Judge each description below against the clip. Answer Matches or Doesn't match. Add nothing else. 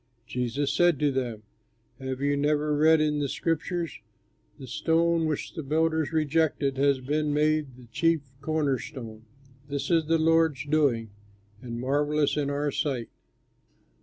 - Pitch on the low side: Doesn't match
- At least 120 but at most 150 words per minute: Matches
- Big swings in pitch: Doesn't match